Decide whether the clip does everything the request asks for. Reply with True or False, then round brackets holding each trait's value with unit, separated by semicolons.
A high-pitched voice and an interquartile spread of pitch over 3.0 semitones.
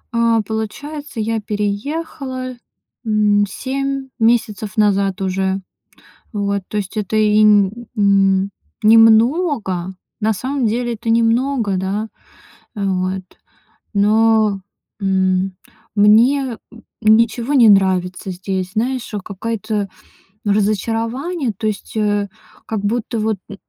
False (215 Hz; 2.7 semitones)